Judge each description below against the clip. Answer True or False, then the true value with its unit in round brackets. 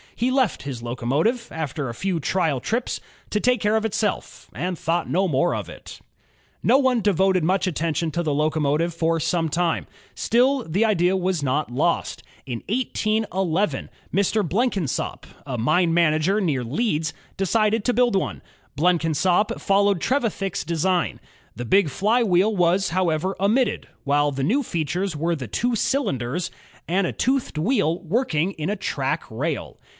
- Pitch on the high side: False (180 Hz)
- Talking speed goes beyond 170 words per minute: False (155 wpm)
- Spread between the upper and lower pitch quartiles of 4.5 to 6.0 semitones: True (5.2 semitones)